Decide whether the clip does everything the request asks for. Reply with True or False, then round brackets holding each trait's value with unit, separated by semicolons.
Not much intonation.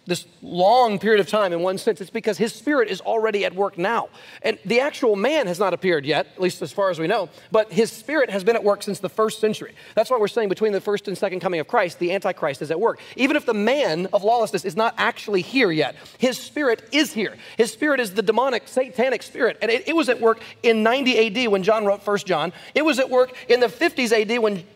False (3.7 semitones)